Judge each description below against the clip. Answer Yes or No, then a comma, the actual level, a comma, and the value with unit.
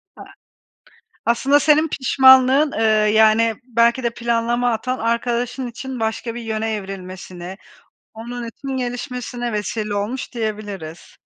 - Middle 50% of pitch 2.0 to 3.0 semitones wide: Yes, narrow, 2.5 semitones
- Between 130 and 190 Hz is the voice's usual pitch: No, high, 235 Hz